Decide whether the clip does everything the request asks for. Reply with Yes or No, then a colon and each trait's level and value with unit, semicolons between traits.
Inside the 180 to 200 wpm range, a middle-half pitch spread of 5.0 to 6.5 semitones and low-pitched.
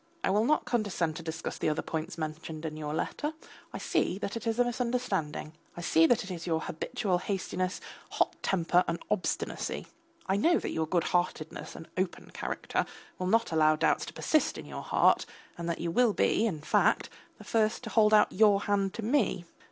No: average, 195 wpm; average, 5.3 semitones; medium, 185 Hz